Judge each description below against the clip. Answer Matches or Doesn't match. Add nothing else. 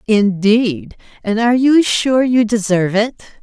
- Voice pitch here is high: Matches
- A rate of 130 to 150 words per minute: Matches